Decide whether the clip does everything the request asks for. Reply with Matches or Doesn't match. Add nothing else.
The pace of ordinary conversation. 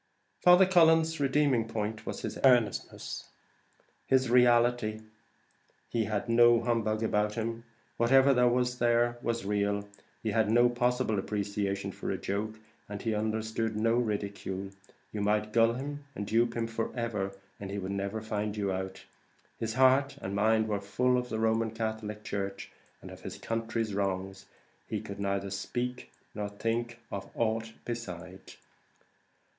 Matches